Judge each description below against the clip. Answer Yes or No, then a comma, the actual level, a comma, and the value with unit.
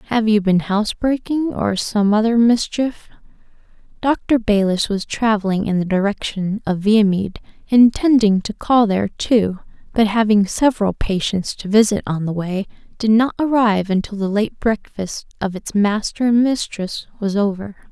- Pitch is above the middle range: Yes, high, 210 Hz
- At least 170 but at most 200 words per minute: No, average, 155 wpm